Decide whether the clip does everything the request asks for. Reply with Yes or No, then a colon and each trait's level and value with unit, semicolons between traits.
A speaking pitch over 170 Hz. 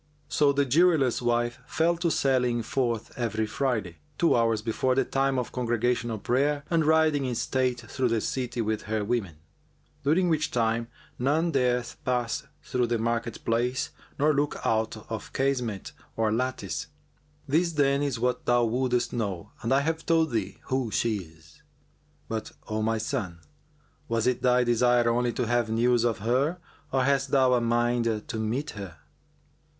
No: low, 120 Hz